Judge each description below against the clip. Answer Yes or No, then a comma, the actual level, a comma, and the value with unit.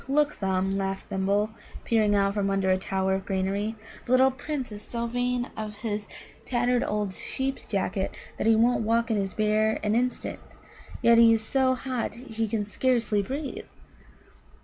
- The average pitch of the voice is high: Yes, high, 220 Hz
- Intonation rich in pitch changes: No, average, 3.7 semitones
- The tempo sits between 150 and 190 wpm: Yes, average, 170 wpm